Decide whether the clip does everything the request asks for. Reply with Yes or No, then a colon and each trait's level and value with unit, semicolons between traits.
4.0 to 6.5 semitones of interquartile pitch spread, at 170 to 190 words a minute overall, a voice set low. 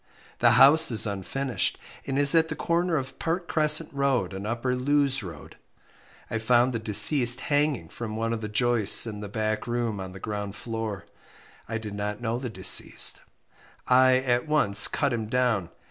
Yes: average, 4.4 semitones; average, 175 wpm; low, 120 Hz